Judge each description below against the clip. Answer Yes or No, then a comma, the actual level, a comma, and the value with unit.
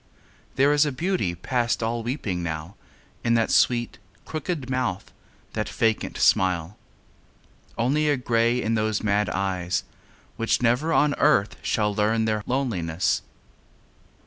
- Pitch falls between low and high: No, low, 115 Hz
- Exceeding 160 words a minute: No, slow, 135 wpm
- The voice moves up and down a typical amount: Yes, average, 4.4 semitones